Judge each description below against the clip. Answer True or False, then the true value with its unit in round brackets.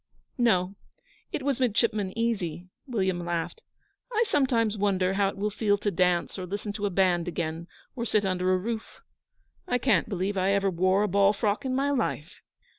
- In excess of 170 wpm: True (190 wpm)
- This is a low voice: False (200 Hz)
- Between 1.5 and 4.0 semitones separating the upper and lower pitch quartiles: True (3.6 semitones)